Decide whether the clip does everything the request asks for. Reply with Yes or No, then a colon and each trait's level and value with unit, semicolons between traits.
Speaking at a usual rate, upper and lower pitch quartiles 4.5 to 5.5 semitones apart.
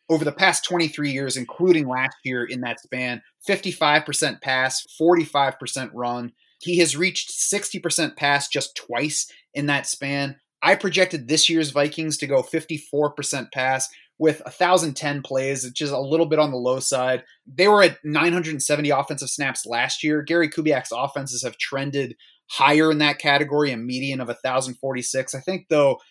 No: average, 160 wpm; average, 3.2 semitones